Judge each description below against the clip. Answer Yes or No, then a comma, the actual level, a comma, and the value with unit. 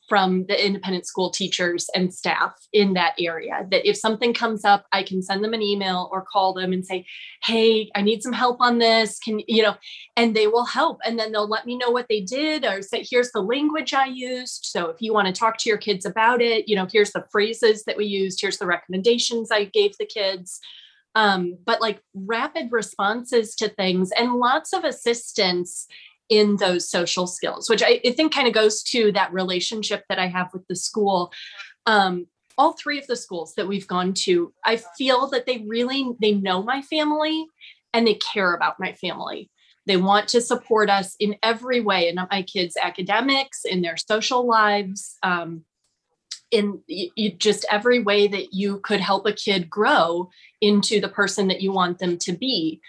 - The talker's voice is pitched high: Yes, high, 210 Hz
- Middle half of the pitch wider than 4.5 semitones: No, average, 3.7 semitones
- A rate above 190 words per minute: Yes, average, 200 wpm